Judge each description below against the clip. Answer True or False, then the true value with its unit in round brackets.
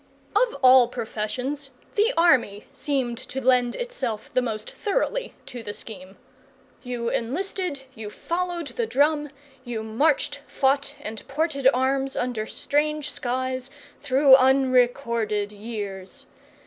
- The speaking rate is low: True (120 wpm)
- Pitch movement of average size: True (3.9 semitones)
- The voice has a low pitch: False (260 Hz)